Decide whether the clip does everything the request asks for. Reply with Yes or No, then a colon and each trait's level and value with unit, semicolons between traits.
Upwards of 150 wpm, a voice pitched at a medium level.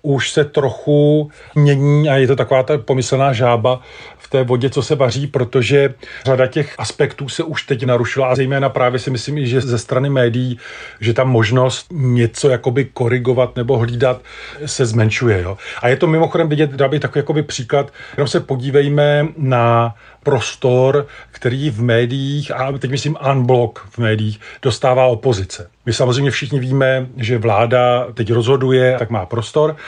No: average, 165 wpm; low, 130 Hz